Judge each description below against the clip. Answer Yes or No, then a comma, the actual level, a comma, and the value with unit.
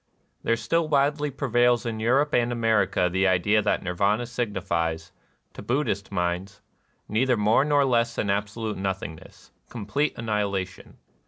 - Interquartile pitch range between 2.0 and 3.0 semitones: No, average, 4.0 semitones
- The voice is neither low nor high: No, low, 110 Hz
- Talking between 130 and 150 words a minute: Yes, average, 140 wpm